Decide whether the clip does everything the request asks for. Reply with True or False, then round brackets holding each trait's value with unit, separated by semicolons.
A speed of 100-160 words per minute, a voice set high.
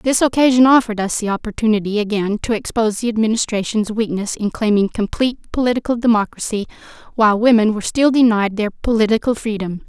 True (150 wpm; 220 Hz)